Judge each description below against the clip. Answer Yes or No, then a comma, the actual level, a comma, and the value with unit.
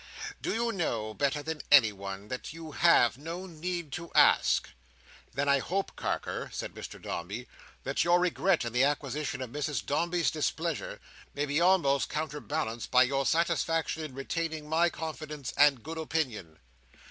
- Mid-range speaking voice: Yes, medium, 150 Hz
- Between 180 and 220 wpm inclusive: No, average, 155 wpm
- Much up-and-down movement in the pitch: No, average, 3.9 semitones